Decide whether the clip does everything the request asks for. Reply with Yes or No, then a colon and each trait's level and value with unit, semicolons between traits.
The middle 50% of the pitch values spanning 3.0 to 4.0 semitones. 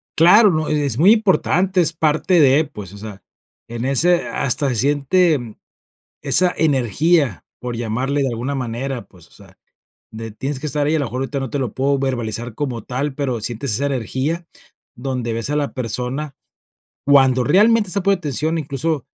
No: average, 4.4 semitones